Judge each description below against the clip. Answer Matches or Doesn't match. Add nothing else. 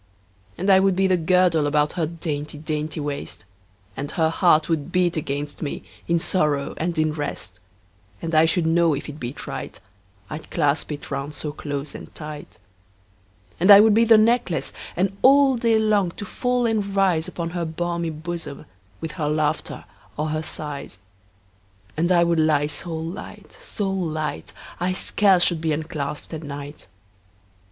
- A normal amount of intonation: Matches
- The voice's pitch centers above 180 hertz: Doesn't match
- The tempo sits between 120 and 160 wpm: Doesn't match